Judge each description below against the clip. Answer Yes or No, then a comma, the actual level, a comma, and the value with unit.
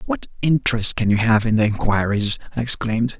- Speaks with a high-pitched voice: No, low, 115 Hz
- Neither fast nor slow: Yes, average, 190 wpm